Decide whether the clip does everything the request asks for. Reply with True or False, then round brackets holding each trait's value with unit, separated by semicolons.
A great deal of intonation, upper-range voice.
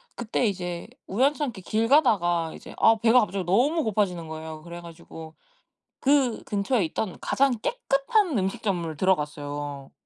True (6.9 semitones; 195 Hz)